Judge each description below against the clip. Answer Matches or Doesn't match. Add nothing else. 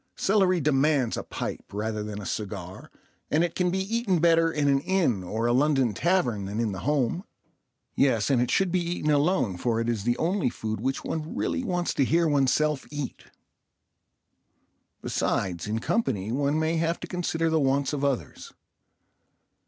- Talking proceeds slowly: Doesn't match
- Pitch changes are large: Matches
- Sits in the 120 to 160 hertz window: Matches